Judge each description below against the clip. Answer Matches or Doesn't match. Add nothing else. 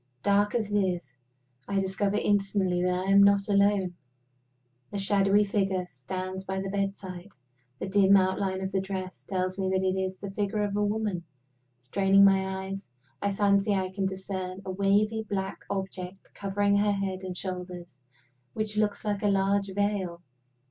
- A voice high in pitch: Matches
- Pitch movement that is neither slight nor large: Doesn't match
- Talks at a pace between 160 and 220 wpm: Matches